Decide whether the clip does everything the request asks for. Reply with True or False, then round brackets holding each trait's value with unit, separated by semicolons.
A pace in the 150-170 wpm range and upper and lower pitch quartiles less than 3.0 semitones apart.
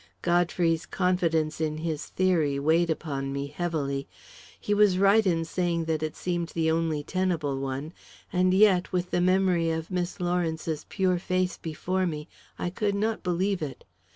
True (160 wpm; 2.6 semitones)